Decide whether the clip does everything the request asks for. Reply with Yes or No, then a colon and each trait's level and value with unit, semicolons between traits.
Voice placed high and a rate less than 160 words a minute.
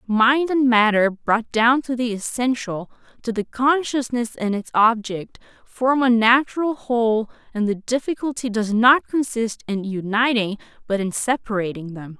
Yes: high, 230 Hz; average, 150 wpm